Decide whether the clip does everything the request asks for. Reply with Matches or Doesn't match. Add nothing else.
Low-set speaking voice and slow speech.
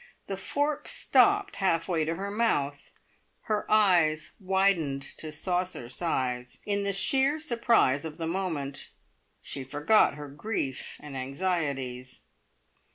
Doesn't match